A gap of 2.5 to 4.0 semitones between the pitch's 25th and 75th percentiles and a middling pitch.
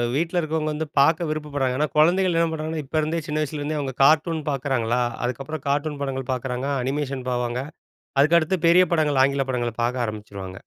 Yes: average, 3.4 semitones; medium, 145 Hz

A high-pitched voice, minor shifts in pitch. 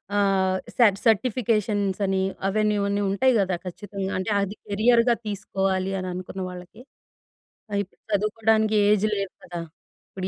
Yes: high, 200 Hz; narrow, 2.0 semitones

